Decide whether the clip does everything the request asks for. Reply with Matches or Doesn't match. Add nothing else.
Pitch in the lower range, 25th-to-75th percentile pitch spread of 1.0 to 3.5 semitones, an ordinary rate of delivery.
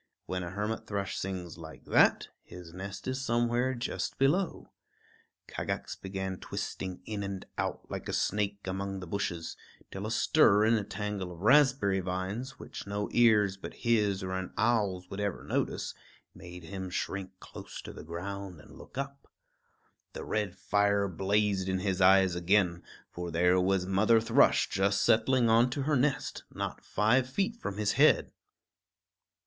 Matches